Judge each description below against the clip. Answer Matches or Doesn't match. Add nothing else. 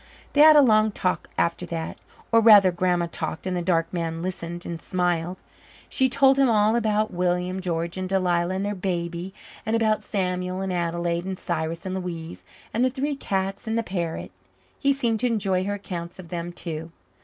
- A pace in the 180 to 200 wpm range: Matches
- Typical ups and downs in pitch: Matches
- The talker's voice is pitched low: Doesn't match